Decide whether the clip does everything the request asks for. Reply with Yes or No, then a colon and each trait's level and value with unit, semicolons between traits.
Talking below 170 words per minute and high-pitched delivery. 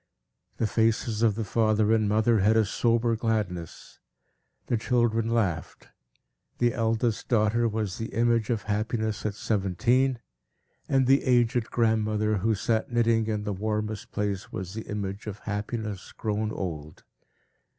No: average, 140 wpm; low, 110 Hz